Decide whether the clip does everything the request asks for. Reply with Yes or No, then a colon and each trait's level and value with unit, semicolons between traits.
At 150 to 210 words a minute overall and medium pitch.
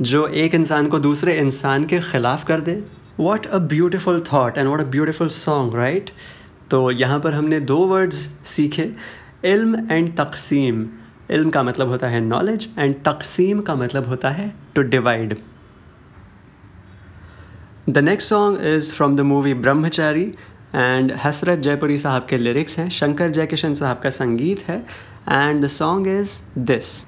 Yes: average, 155 wpm; medium, 145 Hz